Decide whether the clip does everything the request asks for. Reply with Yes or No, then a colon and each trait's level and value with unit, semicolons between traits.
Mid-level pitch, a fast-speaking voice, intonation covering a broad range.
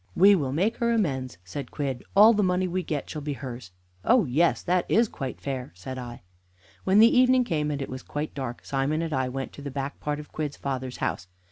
Yes: medium, 145 Hz; fast, 230 wpm; wide, 5.7 semitones